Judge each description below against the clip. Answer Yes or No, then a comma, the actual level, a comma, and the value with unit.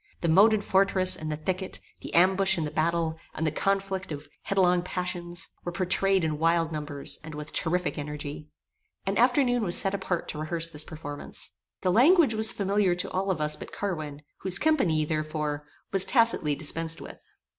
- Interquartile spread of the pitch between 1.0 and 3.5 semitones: No, average, 3.9 semitones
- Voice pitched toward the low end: No, medium, 175 Hz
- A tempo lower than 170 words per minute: No, average, 175 wpm